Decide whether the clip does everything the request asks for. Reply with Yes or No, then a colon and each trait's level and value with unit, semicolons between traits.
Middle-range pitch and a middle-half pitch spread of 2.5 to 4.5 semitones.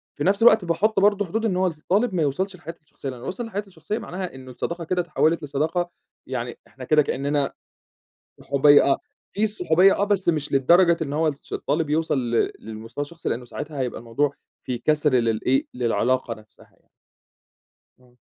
No: medium, 155 Hz; wide, 5.6 semitones